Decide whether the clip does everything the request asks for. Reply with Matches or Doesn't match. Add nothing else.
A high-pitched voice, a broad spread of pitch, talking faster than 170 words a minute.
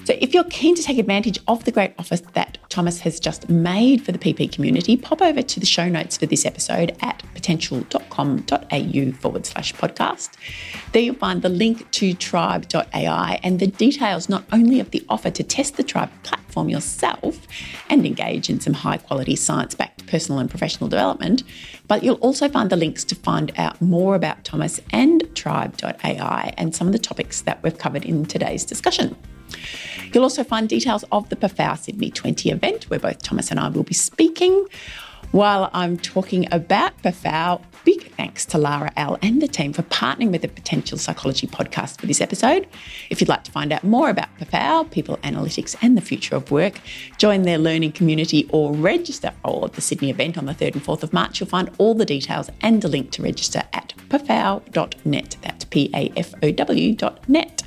Matches